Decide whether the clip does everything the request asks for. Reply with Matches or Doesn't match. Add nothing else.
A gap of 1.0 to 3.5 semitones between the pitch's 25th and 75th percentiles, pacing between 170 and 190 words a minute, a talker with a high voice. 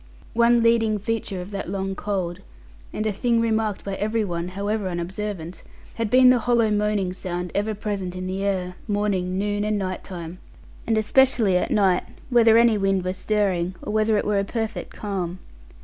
Matches